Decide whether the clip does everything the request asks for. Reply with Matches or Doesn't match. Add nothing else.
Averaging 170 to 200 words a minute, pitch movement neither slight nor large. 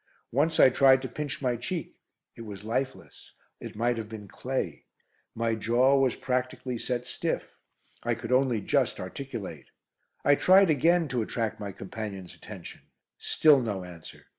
Doesn't match